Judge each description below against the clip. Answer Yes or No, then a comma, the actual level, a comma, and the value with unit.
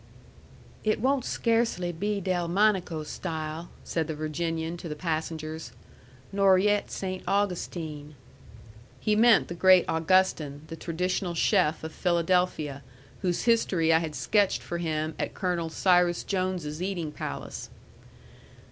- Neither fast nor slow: No, slow, 125 wpm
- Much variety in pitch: No, average, 3.0 semitones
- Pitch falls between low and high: Yes, medium, 175 Hz